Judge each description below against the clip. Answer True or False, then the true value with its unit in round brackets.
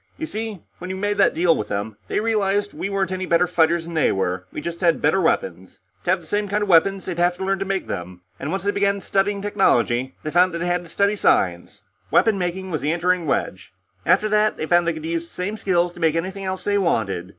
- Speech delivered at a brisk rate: True (260 wpm)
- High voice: False (180 Hz)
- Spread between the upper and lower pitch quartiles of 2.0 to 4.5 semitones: True (3.3 semitones)